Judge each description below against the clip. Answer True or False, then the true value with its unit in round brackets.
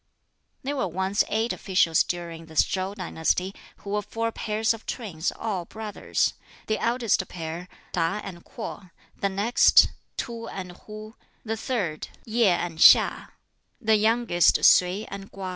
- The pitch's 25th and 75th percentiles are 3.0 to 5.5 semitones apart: True (3.9 semitones)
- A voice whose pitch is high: True (200 Hz)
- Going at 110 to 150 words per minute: True (145 wpm)